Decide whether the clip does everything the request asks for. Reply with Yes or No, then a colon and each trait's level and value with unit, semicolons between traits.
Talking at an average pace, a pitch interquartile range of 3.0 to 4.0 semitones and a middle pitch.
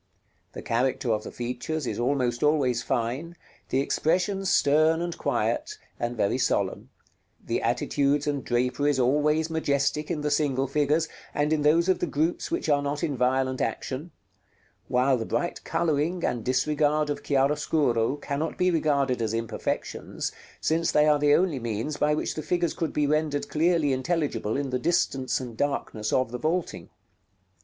Yes: average, 165 wpm; average, 3.4 semitones; medium, 145 Hz